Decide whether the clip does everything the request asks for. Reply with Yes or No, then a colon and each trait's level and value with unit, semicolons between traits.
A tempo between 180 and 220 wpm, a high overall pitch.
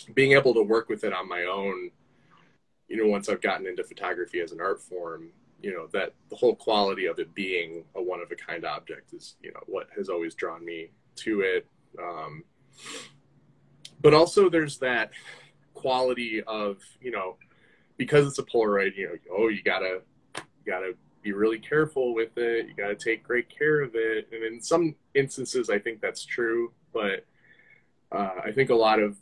No: average, 190 wpm; medium, 140 Hz